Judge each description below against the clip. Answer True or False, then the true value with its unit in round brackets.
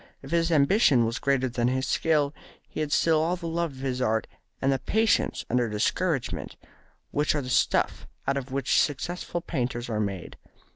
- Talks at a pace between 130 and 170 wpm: False (185 wpm)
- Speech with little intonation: False (4.5 semitones)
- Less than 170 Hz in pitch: True (135 Hz)